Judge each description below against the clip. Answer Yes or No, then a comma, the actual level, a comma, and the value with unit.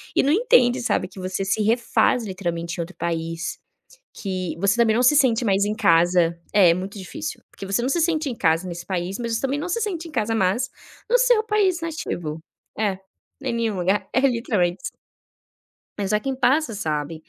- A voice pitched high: Yes, high, 210 Hz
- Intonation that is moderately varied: No, wide, 6.5 semitones